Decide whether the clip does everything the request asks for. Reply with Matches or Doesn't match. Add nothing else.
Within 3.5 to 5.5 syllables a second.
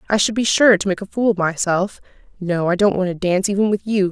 Doesn't match